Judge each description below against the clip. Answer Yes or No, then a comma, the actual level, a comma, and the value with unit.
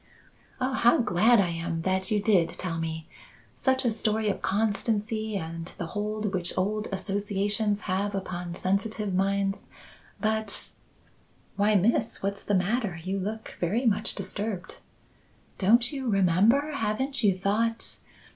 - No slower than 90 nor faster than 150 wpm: Yes, average, 140 wpm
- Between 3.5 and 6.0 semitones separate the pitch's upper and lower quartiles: No, average, 2.8 semitones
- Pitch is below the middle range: No, high, 205 Hz